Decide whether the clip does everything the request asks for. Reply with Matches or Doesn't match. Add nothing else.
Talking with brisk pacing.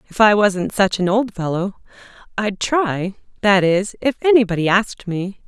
Doesn't match